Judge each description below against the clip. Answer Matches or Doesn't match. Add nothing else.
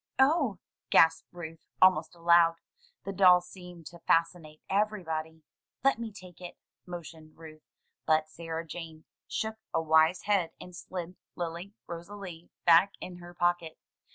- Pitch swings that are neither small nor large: Doesn't match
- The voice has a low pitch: Doesn't match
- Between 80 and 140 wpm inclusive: Matches